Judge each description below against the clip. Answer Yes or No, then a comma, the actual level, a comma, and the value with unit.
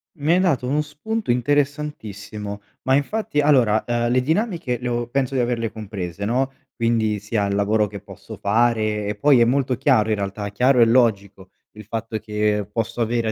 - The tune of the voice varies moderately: Yes, average, 4.1 semitones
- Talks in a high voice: No, low, 115 Hz